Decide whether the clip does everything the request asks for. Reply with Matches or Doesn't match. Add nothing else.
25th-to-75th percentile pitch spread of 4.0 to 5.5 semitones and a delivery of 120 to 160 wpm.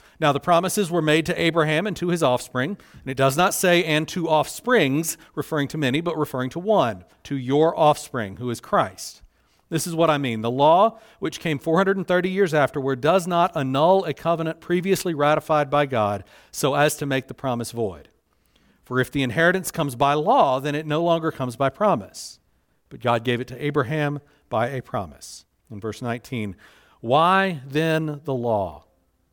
Doesn't match